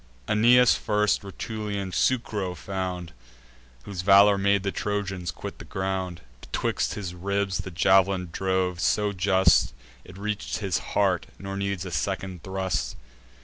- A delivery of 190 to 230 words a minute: No, slow, 135 wpm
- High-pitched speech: No, very low, 95 Hz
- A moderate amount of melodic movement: No, narrow, 1.7 semitones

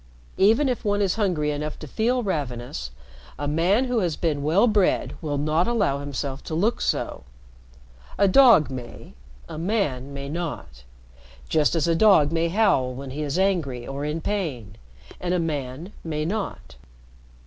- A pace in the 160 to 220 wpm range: Yes, average, 165 wpm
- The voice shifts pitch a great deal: Yes, wide, 5.9 semitones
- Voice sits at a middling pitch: Yes, medium, 160 Hz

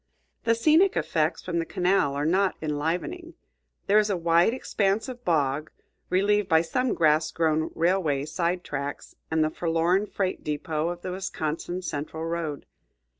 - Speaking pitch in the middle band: Yes, medium, 170 Hz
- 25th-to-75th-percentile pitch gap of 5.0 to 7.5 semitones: No, average, 3.8 semitones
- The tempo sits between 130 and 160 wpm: Yes, average, 155 wpm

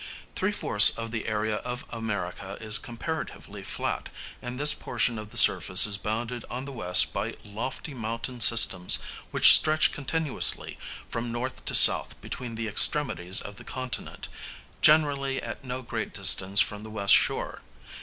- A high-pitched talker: No, low, 115 Hz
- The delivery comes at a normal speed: Yes, average, 155 wpm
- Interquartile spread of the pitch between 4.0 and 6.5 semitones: No, average, 3.4 semitones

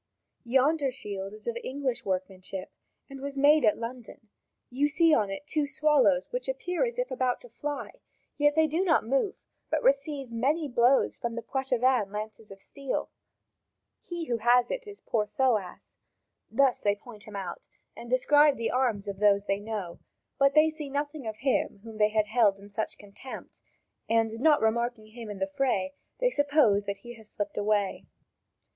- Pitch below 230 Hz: No, high, 245 Hz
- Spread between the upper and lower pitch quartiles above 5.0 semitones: Yes, wide, 5.4 semitones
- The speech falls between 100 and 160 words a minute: No, average, 175 wpm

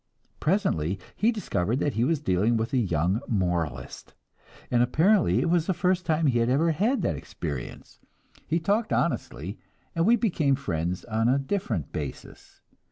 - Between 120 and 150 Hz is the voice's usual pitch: Yes, low, 135 Hz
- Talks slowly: No, average, 165 wpm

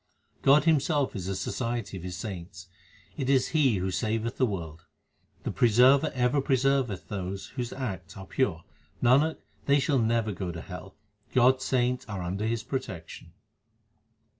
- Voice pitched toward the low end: Yes, low, 115 Hz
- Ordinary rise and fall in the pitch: No, wide, 5.8 semitones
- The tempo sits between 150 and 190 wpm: Yes, average, 160 wpm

